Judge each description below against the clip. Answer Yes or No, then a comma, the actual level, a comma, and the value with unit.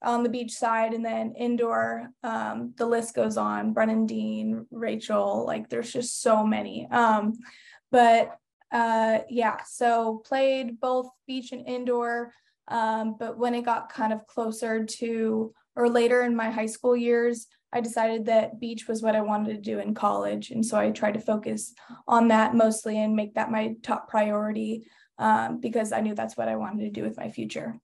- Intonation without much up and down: Yes, narrow, 1.5 semitones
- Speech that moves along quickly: No, average, 185 wpm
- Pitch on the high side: Yes, high, 225 Hz